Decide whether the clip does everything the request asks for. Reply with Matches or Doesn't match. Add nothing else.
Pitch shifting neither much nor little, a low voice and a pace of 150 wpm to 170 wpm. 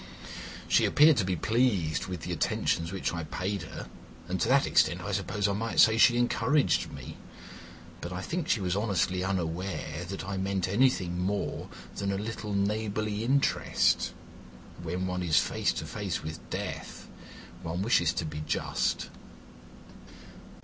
Matches